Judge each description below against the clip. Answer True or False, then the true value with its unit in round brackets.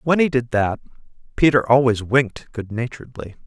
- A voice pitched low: True (125 Hz)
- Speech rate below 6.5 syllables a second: True (5.5 syllables/s)